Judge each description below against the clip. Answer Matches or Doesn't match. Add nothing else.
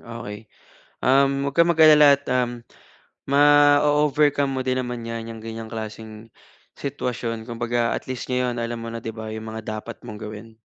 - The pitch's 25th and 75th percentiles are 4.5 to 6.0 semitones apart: Doesn't match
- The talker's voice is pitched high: Doesn't match